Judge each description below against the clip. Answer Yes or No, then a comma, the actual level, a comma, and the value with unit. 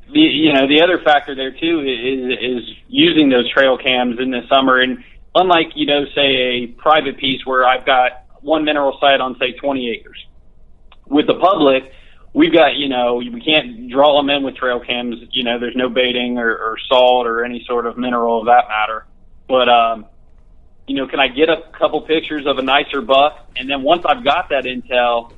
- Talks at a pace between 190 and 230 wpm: Yes, fast, 205 wpm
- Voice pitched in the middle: No, low, 130 Hz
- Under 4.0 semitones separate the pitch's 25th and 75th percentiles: Yes, average, 2.9 semitones